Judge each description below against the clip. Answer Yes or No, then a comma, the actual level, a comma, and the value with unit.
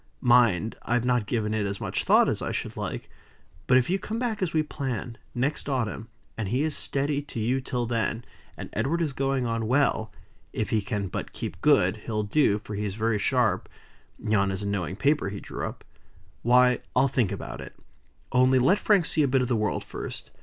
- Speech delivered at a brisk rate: Yes, fast, 210 wpm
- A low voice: Yes, low, 120 Hz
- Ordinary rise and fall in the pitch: Yes, average, 4.3 semitones